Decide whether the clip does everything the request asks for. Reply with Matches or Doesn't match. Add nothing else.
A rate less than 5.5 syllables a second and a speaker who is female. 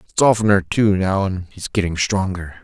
Doesn't match